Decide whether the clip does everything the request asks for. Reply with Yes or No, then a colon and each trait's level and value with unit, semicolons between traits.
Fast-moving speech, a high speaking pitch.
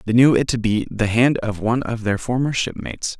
No: fast, 245 wpm; low, 115 Hz